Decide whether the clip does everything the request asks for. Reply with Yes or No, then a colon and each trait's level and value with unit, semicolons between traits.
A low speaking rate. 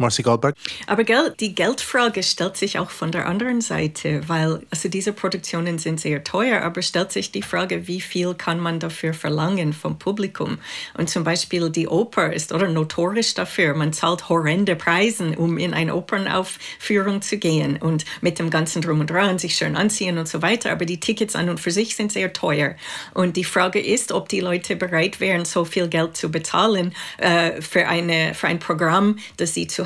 No: fast, 190 wpm